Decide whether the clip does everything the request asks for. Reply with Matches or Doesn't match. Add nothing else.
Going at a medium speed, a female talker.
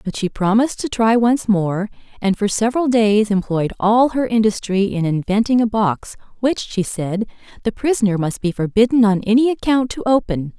Matches